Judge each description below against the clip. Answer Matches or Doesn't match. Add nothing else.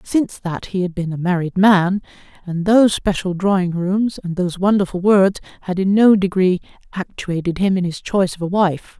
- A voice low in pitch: Doesn't match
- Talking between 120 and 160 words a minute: Doesn't match